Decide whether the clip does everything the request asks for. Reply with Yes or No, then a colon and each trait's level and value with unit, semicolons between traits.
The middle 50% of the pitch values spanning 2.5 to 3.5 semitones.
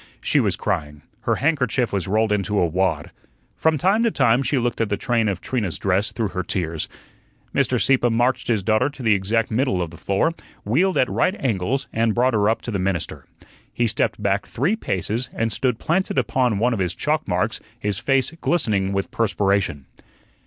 No: average, 4.8 semitones